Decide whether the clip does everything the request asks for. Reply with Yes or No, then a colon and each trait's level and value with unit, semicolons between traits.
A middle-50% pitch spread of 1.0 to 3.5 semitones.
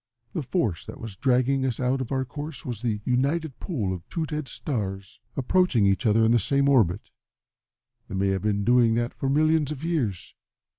No: average, 5.0 semitones